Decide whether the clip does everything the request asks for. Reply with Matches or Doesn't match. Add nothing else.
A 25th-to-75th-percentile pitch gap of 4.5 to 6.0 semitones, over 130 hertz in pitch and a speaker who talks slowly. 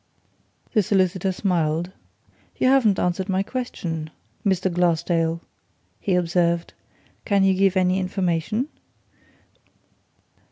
Doesn't match